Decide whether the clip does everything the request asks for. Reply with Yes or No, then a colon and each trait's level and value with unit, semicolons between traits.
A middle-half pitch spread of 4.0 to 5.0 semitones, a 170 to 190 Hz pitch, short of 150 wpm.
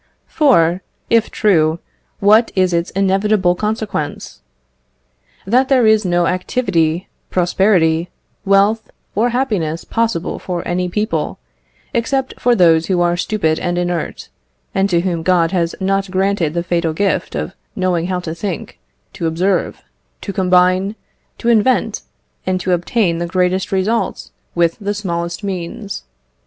No: average, 3.2 semitones; medium, 185 Hz; slow, 135 wpm